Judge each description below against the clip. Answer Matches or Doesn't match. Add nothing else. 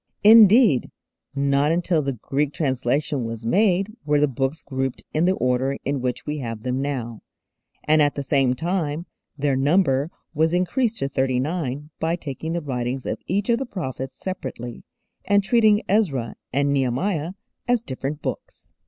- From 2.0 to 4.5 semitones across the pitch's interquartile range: Doesn't match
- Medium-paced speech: Matches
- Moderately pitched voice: Matches